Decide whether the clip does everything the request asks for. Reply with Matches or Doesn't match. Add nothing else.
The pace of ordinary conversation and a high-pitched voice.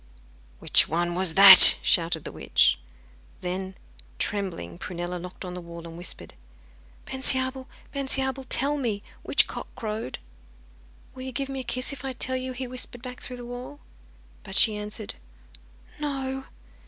Matches